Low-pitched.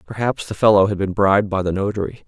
Yes: low, 100 Hz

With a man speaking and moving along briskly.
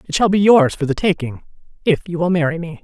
No: female; fast, 235 wpm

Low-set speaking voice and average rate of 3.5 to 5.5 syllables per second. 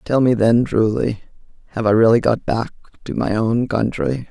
Yes: low, 115 Hz; 4.8 syllables/s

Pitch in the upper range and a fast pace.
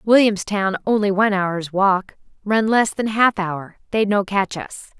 No: high, 200 Hz; average, 170 wpm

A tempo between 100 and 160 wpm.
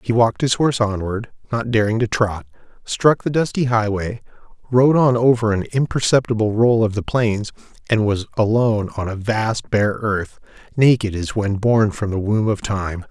No: average, 180 wpm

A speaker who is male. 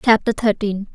No: female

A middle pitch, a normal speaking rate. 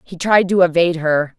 No: medium, 170 Hz; fast, 215 wpm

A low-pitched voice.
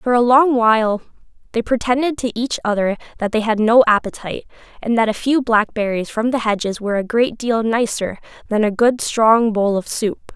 No: high, 225 Hz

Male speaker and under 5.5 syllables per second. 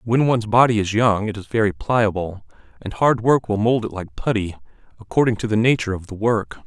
No: male; 5.7 syllables/s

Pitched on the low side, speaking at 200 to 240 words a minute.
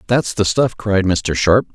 Yes: low, 100 Hz; fast, 205 wpm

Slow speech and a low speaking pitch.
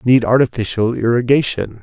Yes: slow, 100 wpm; low, 120 Hz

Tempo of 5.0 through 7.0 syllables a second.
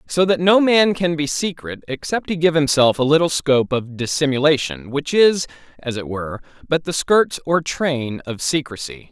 No: 4.8 syllables/s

